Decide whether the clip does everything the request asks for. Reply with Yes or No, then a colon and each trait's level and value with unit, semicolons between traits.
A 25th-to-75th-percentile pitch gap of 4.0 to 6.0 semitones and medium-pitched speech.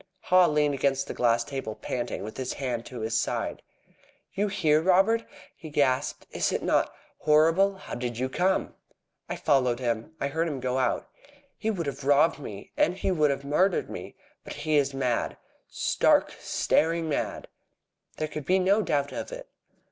Yes: average, 4.8 semitones; medium, 145 Hz